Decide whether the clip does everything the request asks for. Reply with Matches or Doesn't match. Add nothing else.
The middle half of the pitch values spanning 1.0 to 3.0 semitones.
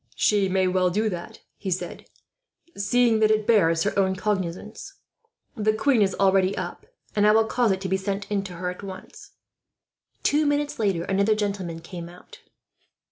Matches